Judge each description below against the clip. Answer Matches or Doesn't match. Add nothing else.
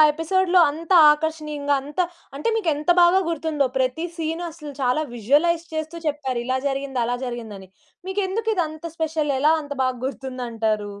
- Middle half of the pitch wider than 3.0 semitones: Matches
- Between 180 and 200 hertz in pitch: Doesn't match